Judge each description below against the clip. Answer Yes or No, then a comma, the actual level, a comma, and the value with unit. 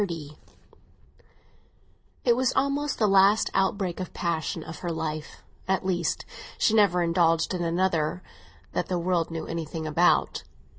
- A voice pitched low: No, medium, 175 Hz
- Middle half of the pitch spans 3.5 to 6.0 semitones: No, average, 2.8 semitones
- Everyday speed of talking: No, slow, 130 wpm